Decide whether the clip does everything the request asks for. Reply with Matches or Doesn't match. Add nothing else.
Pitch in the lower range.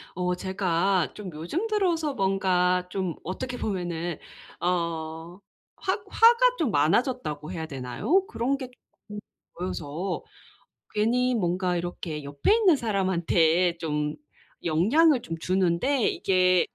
Doesn't match